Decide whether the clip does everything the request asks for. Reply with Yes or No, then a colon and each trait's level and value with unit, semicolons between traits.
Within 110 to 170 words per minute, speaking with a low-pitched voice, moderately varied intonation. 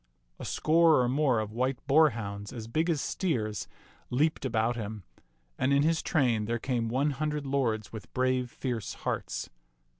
Yes: average, 160 wpm; low, 125 Hz; average, 4.6 semitones